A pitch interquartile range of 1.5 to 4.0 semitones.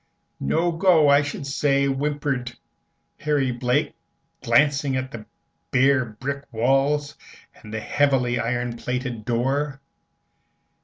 Yes: average, 2.7 semitones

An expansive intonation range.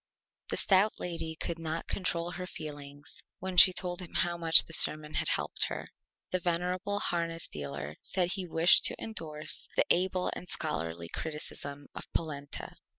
No: average, 3.1 semitones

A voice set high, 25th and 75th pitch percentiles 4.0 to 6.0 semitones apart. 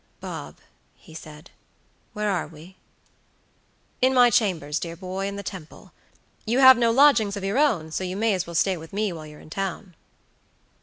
Yes: high, 195 Hz; average, 4.6 semitones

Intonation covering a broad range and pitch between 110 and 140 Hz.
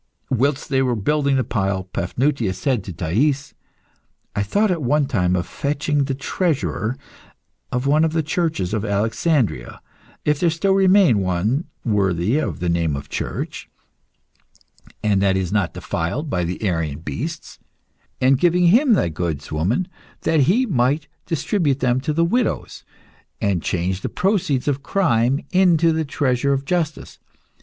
Yes: wide, 8.6 semitones; low, 135 Hz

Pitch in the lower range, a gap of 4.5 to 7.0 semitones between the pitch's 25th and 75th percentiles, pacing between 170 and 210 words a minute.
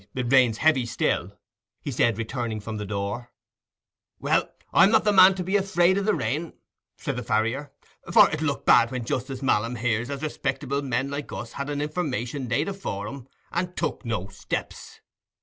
Yes: low, 130 Hz; average, 5.0 semitones; average, 185 wpm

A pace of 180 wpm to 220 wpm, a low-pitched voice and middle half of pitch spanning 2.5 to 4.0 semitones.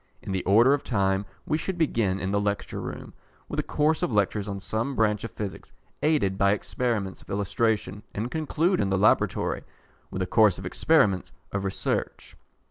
No: average, 185 wpm; low, 105 Hz; average, 4.4 semitones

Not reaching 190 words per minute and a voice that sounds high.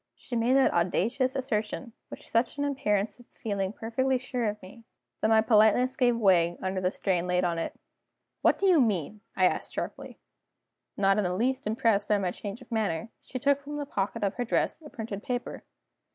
No: average, 200 wpm; high, 220 Hz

